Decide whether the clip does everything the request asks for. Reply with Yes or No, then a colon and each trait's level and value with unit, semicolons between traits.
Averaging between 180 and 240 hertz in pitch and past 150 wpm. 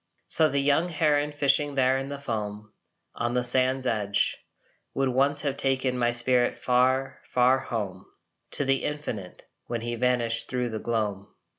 No: low, 125 Hz; average, 160 wpm